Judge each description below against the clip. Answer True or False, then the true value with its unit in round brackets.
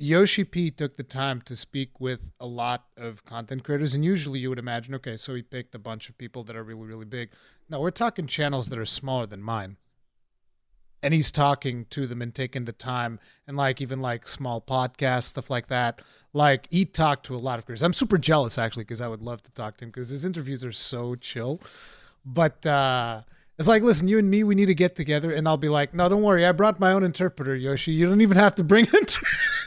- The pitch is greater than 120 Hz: True (135 Hz)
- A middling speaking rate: False (235 wpm)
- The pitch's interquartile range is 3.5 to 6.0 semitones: True (5.0 semitones)